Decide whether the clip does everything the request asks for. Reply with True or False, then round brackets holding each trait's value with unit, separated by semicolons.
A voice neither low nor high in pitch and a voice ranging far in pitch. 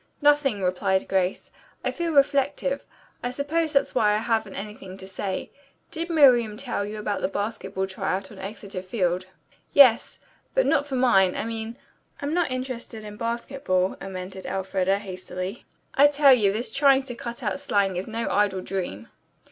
False (215 Hz; 5.9 semitones)